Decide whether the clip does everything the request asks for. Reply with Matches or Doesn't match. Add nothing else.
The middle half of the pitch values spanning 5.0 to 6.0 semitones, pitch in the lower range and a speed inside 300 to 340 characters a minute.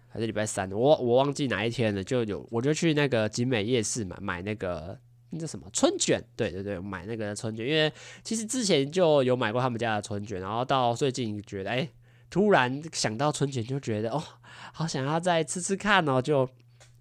Matches